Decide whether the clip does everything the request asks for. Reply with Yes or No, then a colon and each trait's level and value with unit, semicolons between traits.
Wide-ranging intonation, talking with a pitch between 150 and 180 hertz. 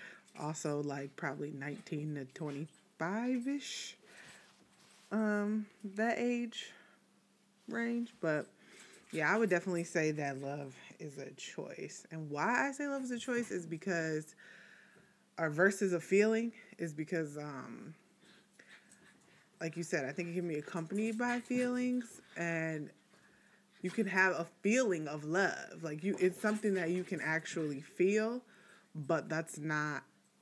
Yes: wide, 5.7 semitones; medium, 175 Hz